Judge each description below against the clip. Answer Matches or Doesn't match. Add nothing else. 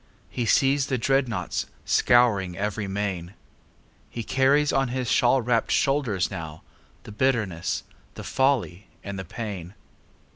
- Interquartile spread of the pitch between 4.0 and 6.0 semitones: Matches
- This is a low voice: Matches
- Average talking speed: Doesn't match